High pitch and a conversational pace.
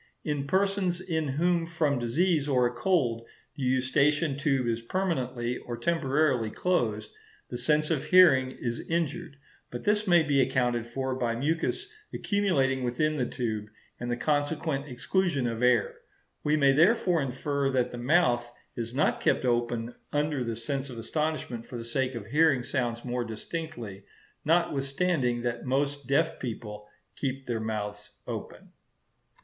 No: low, 135 Hz; average, 150 wpm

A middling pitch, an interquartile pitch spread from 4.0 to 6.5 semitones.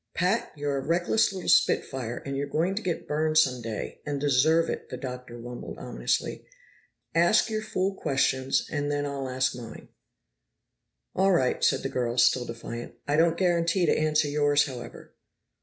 Yes: medium, 145 Hz; average, 4.6 semitones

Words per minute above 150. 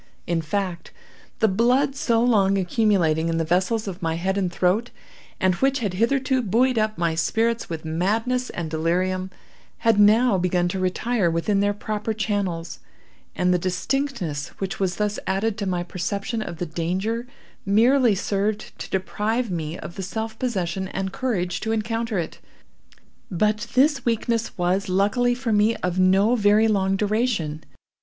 Yes: average, 160 wpm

